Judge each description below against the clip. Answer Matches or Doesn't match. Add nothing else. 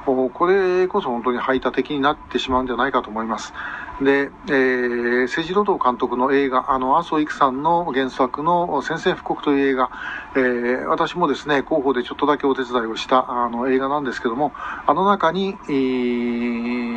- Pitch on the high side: Doesn't match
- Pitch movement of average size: Matches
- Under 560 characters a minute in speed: Matches